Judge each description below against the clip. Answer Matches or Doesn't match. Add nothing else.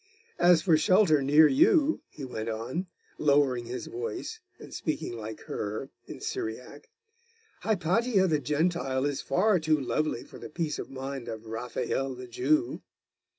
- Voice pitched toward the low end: Doesn't match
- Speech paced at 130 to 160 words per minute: Matches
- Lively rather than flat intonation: Matches